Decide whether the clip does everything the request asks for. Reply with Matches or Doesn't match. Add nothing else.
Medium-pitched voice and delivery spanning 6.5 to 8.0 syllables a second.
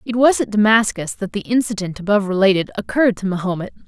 Doesn't match